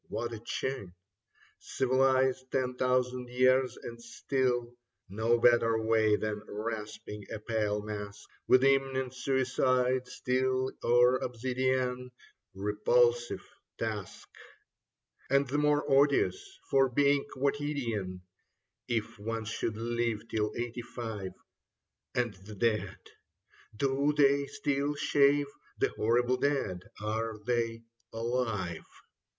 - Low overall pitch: Yes, low, 125 Hz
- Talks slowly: Yes, slow, 110 wpm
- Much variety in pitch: No, average, 3.0 semitones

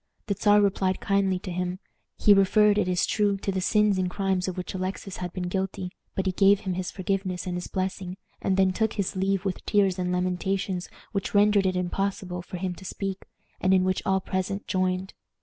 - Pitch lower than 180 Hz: No, high, 190 Hz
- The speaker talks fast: Yes, fast, 210 wpm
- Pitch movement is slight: Yes, narrow, 1.3 semitones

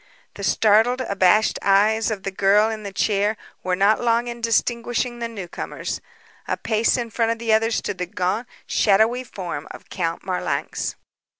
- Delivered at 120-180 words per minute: Yes, average, 170 wpm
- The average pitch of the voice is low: No, high, 220 Hz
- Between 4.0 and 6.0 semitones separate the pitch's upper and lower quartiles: No, average, 2.9 semitones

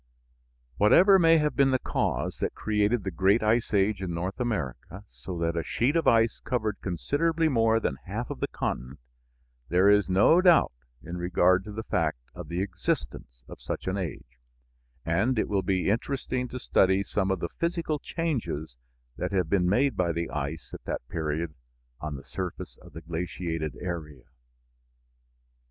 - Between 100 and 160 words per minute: No, average, 175 wpm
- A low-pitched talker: Yes, very low, 95 Hz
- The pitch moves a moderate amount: No, wide, 5.8 semitones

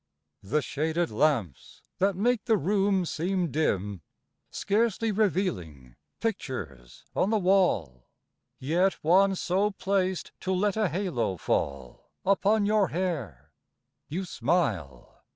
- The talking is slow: Yes, slow, 115 wpm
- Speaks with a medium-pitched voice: Yes, medium, 180 Hz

